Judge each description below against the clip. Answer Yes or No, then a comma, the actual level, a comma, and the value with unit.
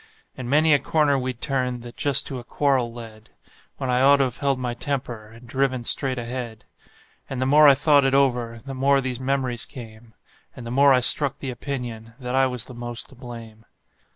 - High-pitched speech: No, low, 130 Hz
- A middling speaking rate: No, fast, 210 wpm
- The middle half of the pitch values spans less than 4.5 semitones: Yes, narrow, 2.4 semitones